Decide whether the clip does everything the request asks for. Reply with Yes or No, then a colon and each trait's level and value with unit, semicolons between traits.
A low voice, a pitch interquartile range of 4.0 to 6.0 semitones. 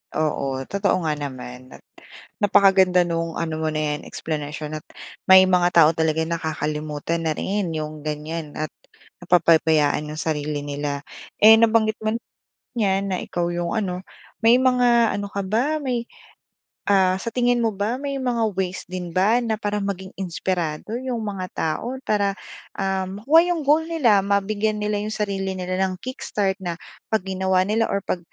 No: high, 190 Hz; average, 5.0 semitones